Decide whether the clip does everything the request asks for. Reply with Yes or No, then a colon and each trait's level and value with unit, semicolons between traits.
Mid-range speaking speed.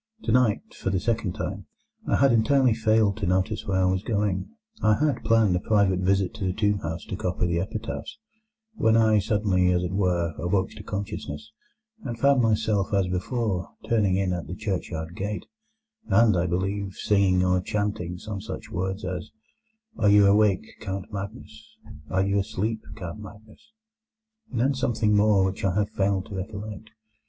Yes: average, 175 wpm